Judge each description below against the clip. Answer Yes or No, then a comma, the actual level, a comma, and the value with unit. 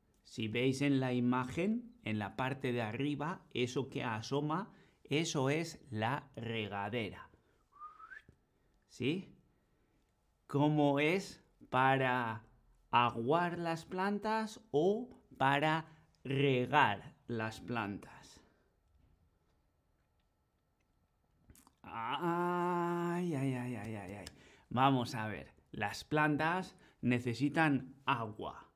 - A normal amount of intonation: No, wide, 6.1 semitones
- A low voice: Yes, low, 130 Hz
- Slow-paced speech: Yes, slow, 90 wpm